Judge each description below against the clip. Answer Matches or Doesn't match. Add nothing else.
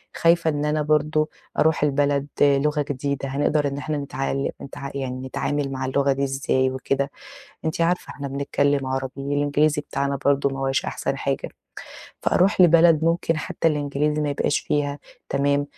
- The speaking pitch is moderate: Matches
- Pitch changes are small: Matches